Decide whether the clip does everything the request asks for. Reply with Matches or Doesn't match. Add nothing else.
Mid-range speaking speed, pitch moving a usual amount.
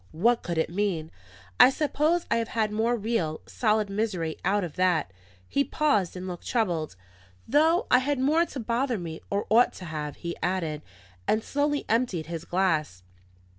Doesn't match